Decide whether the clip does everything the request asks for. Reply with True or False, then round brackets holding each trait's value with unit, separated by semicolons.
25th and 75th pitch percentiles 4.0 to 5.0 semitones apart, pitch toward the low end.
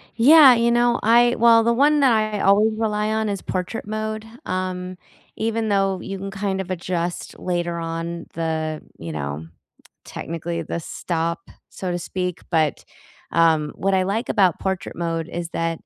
False (4.5 semitones; 185 Hz)